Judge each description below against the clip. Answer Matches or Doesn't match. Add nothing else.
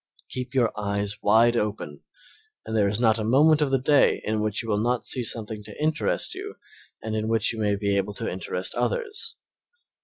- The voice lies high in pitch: Doesn't match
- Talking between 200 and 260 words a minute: Matches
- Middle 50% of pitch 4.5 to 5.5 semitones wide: Doesn't match